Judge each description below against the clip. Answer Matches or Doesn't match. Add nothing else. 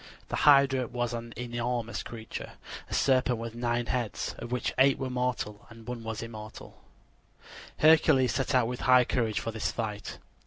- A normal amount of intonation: Doesn't match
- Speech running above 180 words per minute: Doesn't match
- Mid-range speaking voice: Doesn't match